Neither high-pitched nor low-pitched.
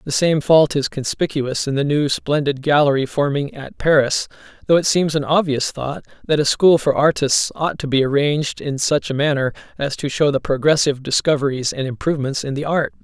Yes: medium, 145 Hz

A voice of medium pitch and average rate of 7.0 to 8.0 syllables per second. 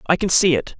No: medium, 175 Hz; 6.2 syllables/s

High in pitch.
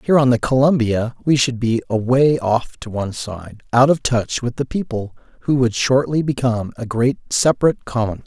No: low, 125 Hz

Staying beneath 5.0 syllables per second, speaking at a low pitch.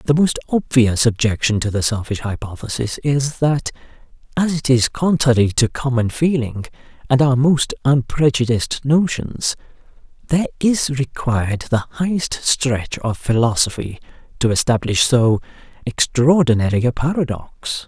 Yes: 4.5 syllables/s; low, 130 Hz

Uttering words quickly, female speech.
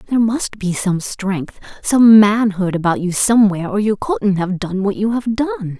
No: average, 195 wpm; female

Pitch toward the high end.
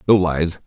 No: very low, 85 Hz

